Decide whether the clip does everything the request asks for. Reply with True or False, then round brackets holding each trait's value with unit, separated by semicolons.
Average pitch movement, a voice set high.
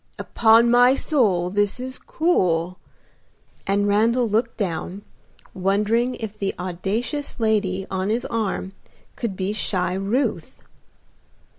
True (3.7 semitones; 205 Hz)